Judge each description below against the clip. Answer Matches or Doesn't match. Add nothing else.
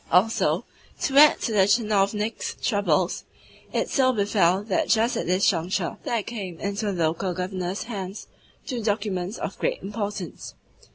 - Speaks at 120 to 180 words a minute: Matches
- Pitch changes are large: Doesn't match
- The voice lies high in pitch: Matches